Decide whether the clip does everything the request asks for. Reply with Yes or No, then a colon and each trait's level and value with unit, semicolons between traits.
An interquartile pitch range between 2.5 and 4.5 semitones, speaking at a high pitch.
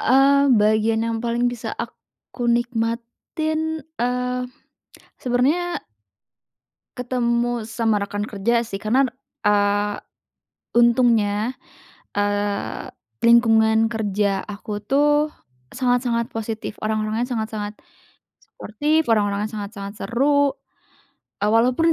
Yes: average, 2.9 semitones; high, 230 Hz